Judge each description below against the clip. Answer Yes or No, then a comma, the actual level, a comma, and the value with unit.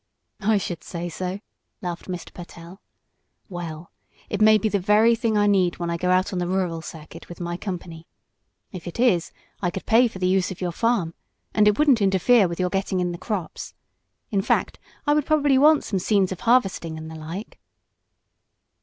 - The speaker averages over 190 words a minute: Yes, average, 200 wpm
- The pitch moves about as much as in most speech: Yes, average, 3.5 semitones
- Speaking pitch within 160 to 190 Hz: Yes, medium, 185 Hz